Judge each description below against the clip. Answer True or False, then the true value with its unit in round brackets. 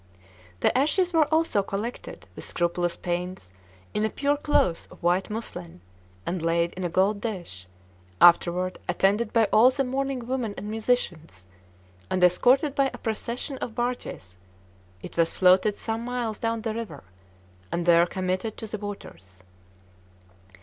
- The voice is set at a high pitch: True (210 Hz)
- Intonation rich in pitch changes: True (5.7 semitones)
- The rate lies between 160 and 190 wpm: False (150 wpm)